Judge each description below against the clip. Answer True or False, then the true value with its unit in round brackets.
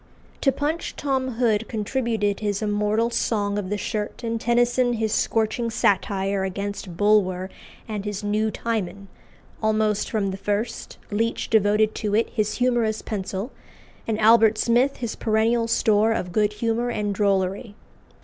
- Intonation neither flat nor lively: False (2.0 semitones)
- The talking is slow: False (145 wpm)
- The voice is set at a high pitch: True (215 Hz)